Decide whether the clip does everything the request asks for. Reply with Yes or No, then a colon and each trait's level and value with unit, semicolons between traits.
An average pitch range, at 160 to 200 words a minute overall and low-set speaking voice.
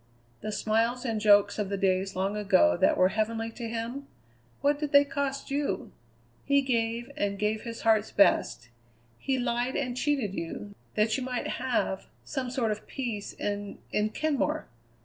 No: average, 3.9 semitones; average, 170 wpm; high, 225 Hz